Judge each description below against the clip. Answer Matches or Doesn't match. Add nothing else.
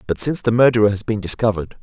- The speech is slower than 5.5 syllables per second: Doesn't match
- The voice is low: Matches